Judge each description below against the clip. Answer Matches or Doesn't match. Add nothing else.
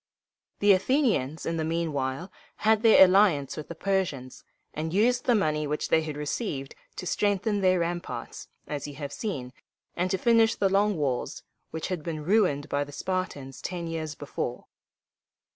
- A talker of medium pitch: Matches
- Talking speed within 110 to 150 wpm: Doesn't match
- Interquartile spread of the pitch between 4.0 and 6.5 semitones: Matches